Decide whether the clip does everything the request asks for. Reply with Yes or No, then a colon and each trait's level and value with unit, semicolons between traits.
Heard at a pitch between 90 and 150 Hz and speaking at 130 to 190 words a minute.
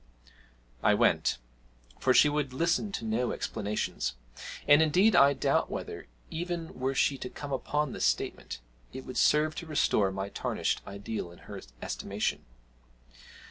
Yes: low, 135 Hz; average, 145 wpm